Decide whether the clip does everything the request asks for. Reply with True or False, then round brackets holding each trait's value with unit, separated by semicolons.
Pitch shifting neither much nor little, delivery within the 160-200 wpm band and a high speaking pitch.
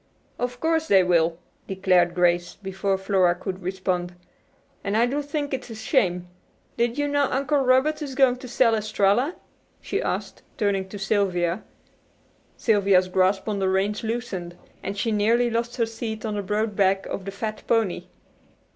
True (4.2 semitones; 165 wpm; 205 Hz)